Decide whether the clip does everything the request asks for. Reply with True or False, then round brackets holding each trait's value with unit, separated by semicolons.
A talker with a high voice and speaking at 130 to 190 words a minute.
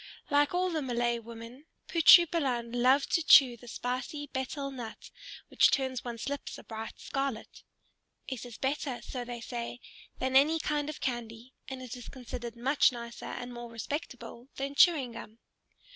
True (255 Hz; 165 wpm)